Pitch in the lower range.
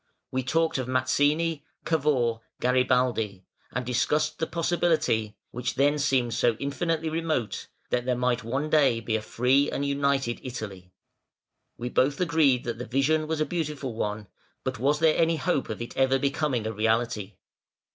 Yes: low, 130 Hz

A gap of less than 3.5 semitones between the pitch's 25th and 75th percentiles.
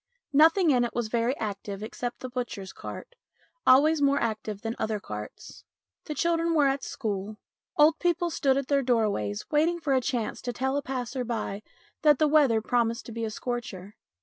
No: average, 4.9 semitones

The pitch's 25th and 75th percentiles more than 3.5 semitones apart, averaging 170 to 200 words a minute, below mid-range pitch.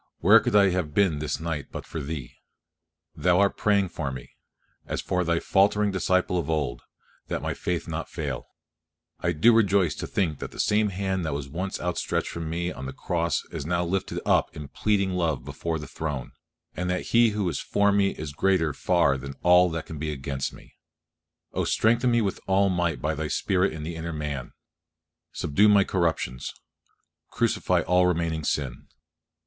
Yes: average, 4.1 semitones; average, 185 wpm; very low, 85 Hz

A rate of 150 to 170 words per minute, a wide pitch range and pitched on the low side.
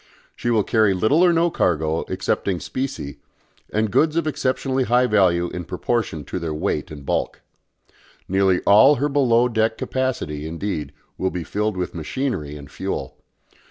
Yes: average, 160 wpm; wide, 7.1 semitones; low, 105 Hz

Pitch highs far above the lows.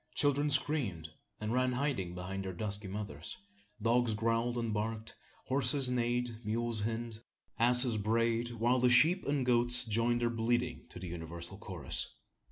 No: average, 2.8 semitones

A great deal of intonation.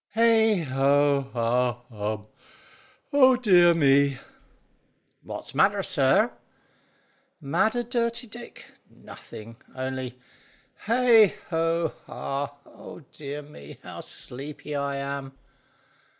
Yes: wide, 8.5 semitones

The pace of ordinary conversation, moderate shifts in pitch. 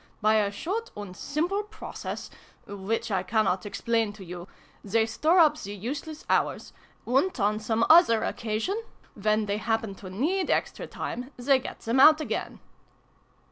No: average, 155 wpm; wide, 6.8 semitones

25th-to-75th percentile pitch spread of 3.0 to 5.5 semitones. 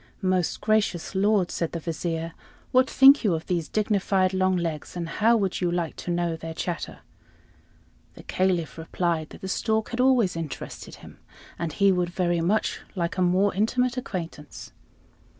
Yes: average, 3.5 semitones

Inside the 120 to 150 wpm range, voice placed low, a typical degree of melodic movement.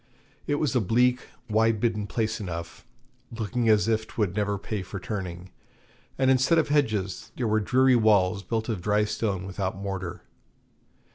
No: average, 160 wpm; low, 110 Hz; average, 3.2 semitones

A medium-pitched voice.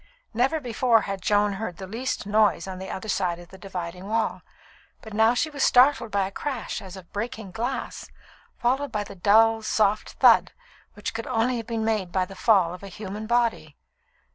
No: high, 215 Hz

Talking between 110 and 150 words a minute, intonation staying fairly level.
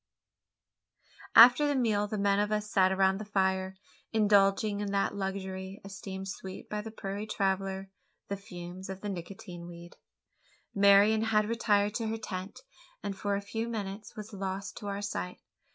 No: average, 165 wpm; narrow, 1.7 semitones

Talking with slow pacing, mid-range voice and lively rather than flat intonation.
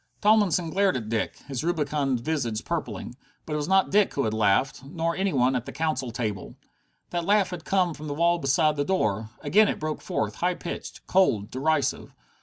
No: average, 200 wpm; medium, 155 Hz; wide, 6.0 semitones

